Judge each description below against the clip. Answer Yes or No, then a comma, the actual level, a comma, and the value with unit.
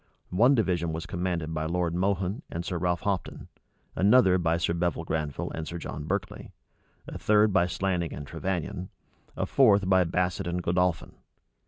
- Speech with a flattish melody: Yes, narrow, 2.2 semitones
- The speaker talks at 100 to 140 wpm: No, average, 165 wpm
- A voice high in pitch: No, very low, 90 Hz